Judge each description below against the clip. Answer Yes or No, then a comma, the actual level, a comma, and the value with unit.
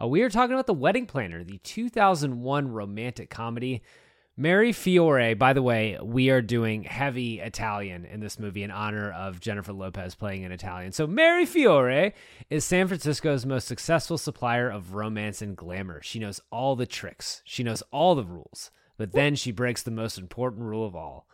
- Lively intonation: Yes, wide, 5.7 semitones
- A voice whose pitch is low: Yes, low, 120 Hz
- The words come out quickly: No, average, 185 wpm